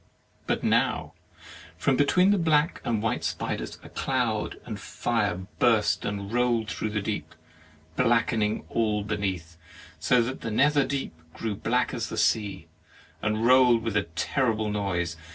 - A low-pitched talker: Yes, low, 110 Hz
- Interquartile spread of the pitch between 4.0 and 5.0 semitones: No, average, 3.2 semitones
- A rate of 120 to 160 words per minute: Yes, average, 150 wpm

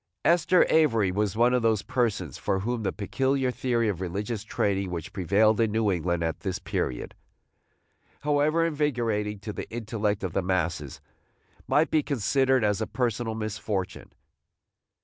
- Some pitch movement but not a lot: Yes, average, 4.5 semitones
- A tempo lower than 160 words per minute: Yes, average, 150 wpm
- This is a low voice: Yes, low, 110 Hz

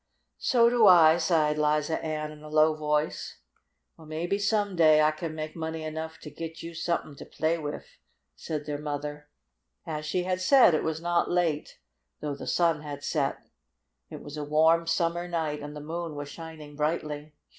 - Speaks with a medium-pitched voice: Yes, medium, 155 Hz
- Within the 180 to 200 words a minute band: Yes, average, 185 wpm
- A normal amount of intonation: No, narrow, 1.9 semitones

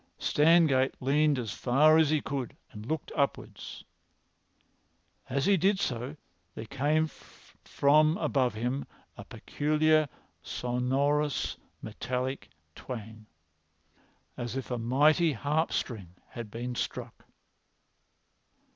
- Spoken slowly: Yes, slow, 105 wpm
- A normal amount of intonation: Yes, average, 3.8 semitones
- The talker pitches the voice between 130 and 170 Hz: Yes, low, 135 Hz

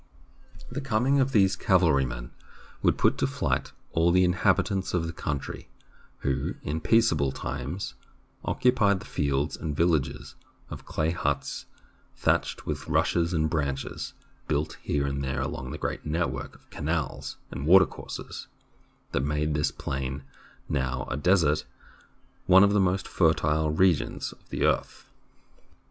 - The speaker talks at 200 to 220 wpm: No, average, 140 wpm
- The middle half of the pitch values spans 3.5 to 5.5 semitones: Yes, average, 4.7 semitones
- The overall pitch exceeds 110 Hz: No, very low, 80 Hz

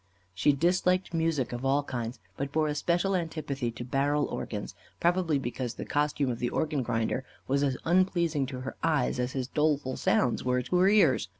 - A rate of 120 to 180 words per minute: No, average, 190 wpm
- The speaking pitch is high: No, medium, 140 Hz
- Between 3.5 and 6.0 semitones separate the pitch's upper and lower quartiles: Yes, average, 4.4 semitones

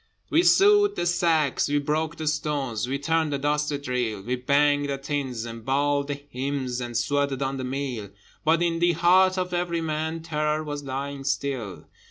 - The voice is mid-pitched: Yes, medium, 145 Hz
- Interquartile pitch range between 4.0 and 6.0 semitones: No, average, 3.1 semitones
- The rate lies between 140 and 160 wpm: No, average, 185 wpm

